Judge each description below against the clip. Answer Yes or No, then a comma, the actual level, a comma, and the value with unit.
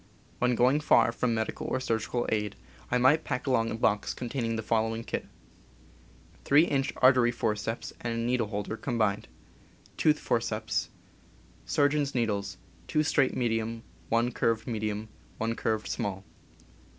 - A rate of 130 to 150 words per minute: Yes, average, 140 wpm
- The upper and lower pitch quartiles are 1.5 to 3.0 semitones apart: Yes, narrow, 2.4 semitones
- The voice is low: Yes, low, 115 Hz